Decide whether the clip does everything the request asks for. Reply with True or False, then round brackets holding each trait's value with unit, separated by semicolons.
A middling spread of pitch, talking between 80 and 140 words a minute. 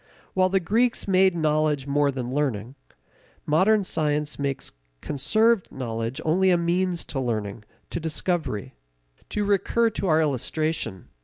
False (5.7 semitones; 135 wpm)